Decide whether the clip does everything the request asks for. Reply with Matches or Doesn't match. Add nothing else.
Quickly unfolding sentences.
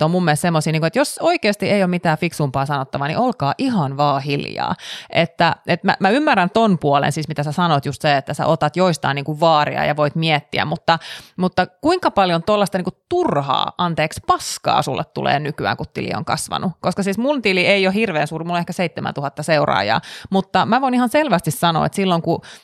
Matches